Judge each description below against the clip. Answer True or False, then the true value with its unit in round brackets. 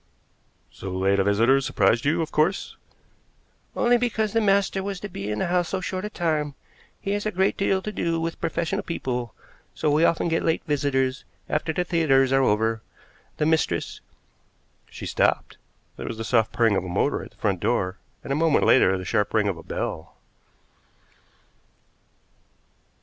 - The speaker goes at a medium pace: True (180 wpm)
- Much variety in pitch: True (8.1 semitones)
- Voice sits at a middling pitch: True (150 Hz)